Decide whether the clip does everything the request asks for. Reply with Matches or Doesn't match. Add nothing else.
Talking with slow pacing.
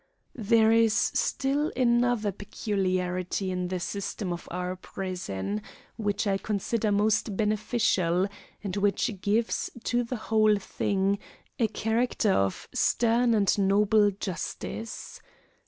Matches